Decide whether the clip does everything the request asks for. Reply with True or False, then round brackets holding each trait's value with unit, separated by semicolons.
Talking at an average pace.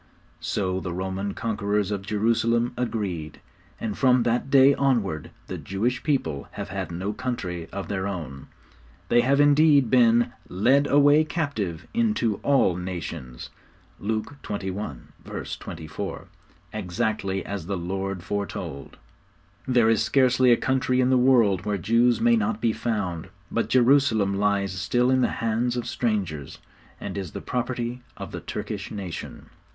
True (145 wpm)